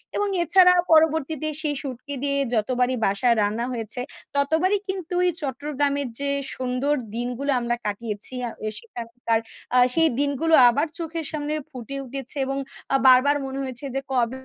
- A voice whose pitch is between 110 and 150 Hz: No, very high, 275 Hz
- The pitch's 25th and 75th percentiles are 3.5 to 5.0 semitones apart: Yes, average, 3.8 semitones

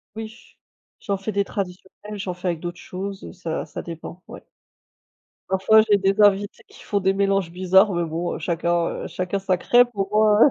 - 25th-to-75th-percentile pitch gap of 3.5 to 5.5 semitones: No, narrow, 2.4 semitones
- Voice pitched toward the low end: No, high, 190 Hz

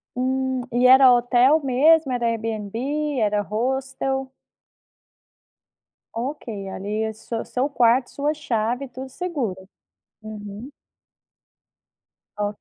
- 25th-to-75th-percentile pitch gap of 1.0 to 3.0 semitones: No, average, 3.4 semitones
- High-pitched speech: Yes, high, 245 Hz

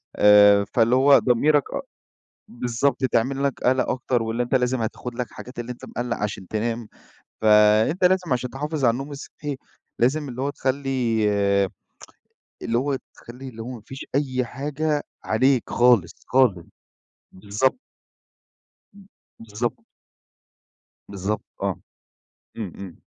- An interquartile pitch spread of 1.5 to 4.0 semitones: Yes, average, 3.3 semitones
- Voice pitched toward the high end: No, low, 125 Hz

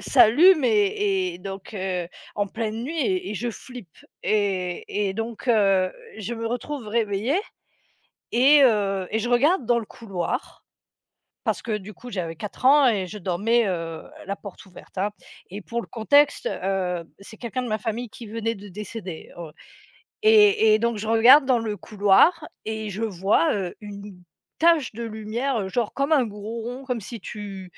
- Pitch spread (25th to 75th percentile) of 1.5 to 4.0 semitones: Yes, average, 3.6 semitones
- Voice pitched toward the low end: No, high, 215 Hz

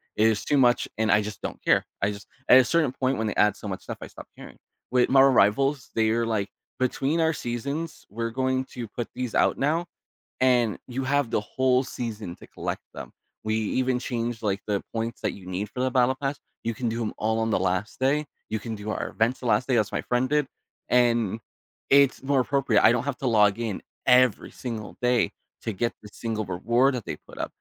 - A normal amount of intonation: Yes, average, 3.3 semitones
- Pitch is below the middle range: Yes, low, 120 Hz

